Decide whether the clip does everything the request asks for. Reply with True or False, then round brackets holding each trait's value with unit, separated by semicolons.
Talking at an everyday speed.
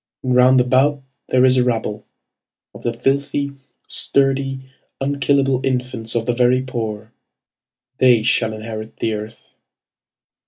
False (125 wpm)